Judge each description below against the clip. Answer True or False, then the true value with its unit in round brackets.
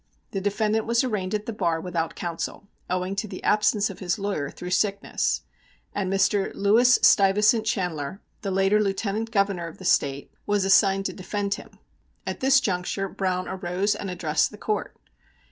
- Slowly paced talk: False (170 wpm)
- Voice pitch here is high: True (195 Hz)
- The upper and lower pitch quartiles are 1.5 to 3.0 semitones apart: True (2.4 semitones)